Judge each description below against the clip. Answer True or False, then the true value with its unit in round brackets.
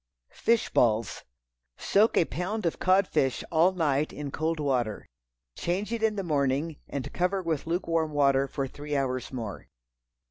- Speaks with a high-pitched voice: False (155 Hz)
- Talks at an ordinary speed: True (155 wpm)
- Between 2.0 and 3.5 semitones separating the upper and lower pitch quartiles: False (4.7 semitones)